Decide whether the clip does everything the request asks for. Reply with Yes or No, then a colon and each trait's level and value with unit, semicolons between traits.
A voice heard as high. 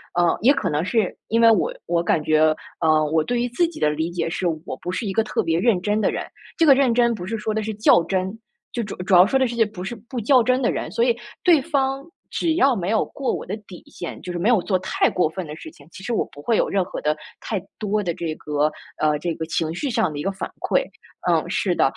Yes: high, 200 Hz